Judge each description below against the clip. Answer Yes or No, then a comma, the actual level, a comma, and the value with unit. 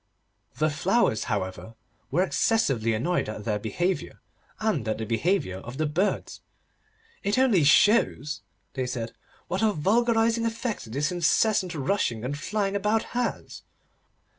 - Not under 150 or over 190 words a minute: No, slow, 135 wpm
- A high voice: No, medium, 170 Hz